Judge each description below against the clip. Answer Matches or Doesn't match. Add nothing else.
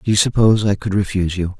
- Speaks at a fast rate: Matches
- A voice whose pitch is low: Matches